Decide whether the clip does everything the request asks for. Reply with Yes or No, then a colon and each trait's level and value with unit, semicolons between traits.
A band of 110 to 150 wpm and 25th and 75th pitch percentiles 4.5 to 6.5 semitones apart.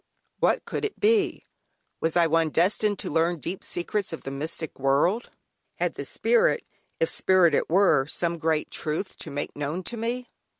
No: average, 175 wpm; average, 5.3 semitones